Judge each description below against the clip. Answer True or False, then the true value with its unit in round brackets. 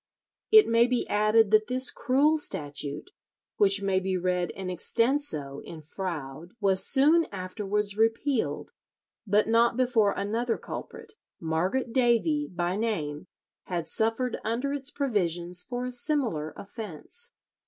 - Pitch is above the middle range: True (215 Hz)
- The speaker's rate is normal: False (130 wpm)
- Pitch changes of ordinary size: False (5.7 semitones)